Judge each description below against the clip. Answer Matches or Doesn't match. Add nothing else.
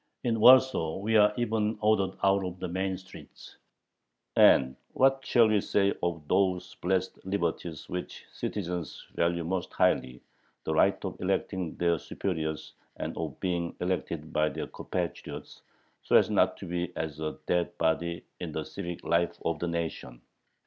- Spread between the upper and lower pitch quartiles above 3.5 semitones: Doesn't match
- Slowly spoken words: Doesn't match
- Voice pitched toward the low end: Matches